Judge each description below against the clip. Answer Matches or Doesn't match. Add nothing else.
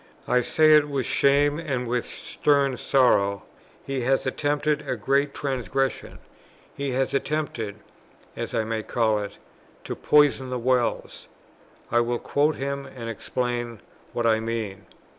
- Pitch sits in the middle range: Doesn't match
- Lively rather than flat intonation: Doesn't match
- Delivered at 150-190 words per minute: Doesn't match